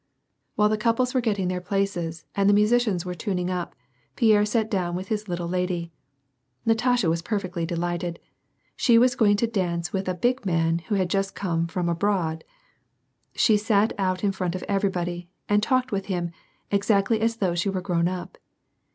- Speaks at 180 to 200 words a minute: Yes, average, 185 wpm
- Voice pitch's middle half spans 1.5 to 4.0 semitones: Yes, average, 3.3 semitones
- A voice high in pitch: Yes, high, 195 Hz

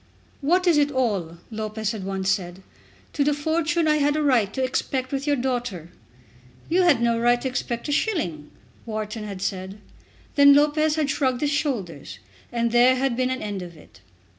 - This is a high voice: Yes, very high, 250 Hz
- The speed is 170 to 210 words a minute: Yes, average, 190 wpm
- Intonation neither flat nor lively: No, wide, 6.1 semitones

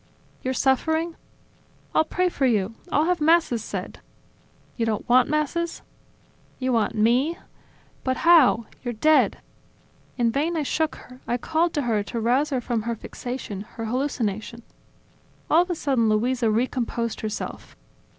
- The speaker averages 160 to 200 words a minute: No, average, 150 wpm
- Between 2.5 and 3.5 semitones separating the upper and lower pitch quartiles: No, average, 5.2 semitones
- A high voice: Yes, very high, 255 Hz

